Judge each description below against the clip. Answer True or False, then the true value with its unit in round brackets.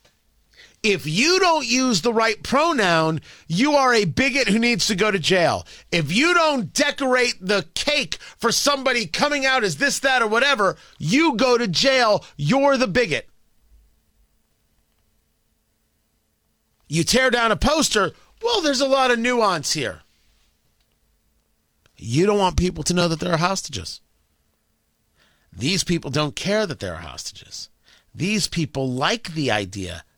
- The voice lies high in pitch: True (200 Hz)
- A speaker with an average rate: True (145 wpm)